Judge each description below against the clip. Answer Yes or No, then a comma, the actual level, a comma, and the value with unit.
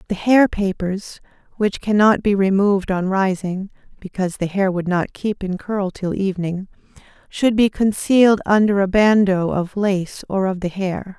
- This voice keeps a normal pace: Yes, average, 165 wpm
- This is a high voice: Yes, high, 195 Hz